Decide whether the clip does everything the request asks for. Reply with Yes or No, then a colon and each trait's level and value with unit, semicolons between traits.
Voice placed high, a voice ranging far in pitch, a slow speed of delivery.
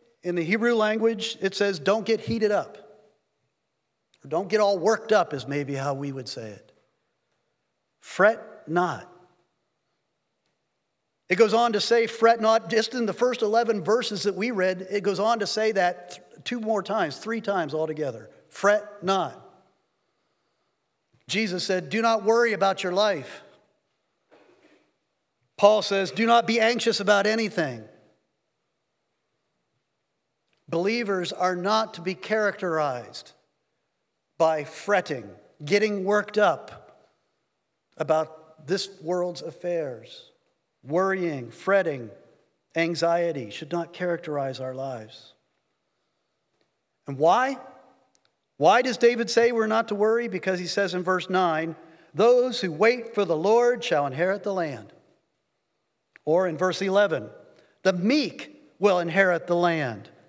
No: high, 195 Hz; average, 4.6 semitones; slow, 130 wpm